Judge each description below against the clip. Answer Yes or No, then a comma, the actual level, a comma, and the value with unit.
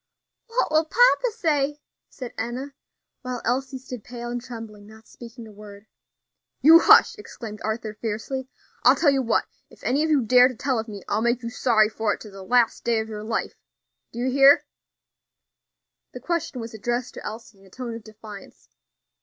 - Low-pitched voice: No, high, 240 Hz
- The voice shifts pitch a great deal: No, average, 3.3 semitones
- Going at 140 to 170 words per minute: No, average, 190 wpm